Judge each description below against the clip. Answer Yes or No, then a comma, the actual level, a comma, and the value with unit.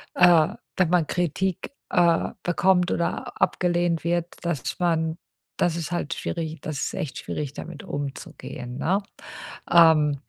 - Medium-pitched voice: Yes, medium, 170 Hz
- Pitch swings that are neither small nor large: No, narrow, 2.2 semitones